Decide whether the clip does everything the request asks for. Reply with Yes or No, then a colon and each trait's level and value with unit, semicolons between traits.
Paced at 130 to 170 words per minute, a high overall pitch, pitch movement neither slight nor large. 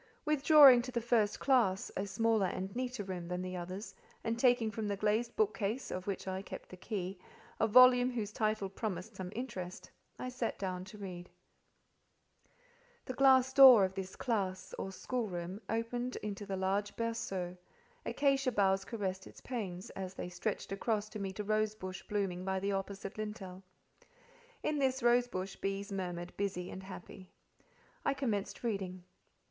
Yes: average, 165 wpm; high, 205 Hz; average, 3.9 semitones